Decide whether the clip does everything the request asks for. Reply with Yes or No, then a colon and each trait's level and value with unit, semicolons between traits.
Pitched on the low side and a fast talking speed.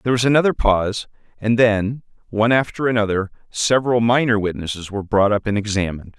No: low, 110 Hz; average, 165 wpm